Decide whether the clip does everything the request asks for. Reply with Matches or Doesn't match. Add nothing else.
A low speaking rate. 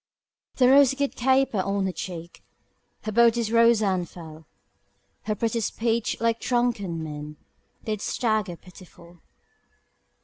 Matches